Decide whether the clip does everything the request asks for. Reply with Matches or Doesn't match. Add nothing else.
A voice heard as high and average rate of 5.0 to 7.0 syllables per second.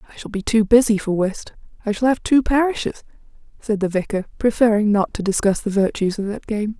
Matches